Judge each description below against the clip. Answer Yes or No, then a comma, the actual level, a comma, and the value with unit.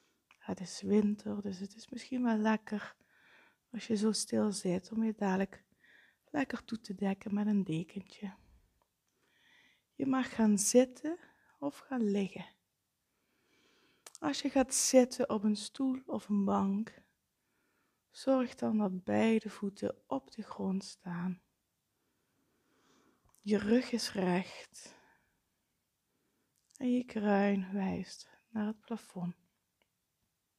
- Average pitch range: Yes, average, 3.6 semitones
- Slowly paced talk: Yes, slow, 120 wpm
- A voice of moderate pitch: No, high, 210 Hz